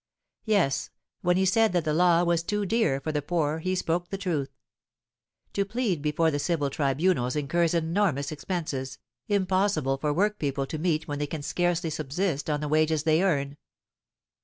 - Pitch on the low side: No, medium, 160 Hz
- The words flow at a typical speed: Yes, average, 170 wpm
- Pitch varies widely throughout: No, average, 3.9 semitones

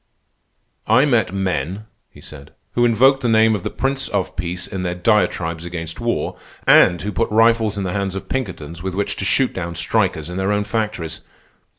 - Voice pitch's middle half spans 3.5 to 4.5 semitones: Yes, average, 4.2 semitones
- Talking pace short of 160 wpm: No, average, 195 wpm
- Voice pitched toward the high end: No, very low, 95 Hz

